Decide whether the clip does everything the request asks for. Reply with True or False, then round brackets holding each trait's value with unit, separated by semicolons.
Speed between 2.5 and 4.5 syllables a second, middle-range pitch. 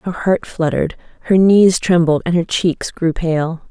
True (4.3 syllables/s; 170 Hz)